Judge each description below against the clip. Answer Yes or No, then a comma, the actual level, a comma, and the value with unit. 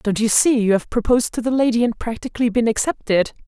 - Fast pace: Yes, fast, 225 wpm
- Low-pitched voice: No, high, 230 Hz